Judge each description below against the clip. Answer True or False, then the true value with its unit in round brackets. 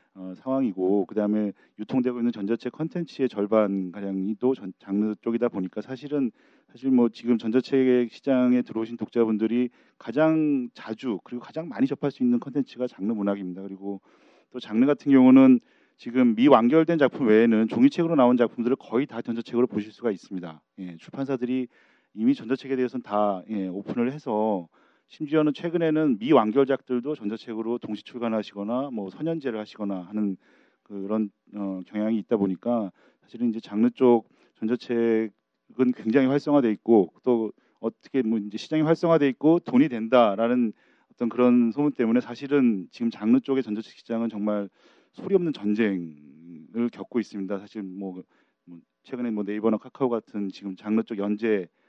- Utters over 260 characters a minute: True (360 characters per minute)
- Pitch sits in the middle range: False (115 Hz)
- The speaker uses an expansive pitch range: False (4.0 semitones)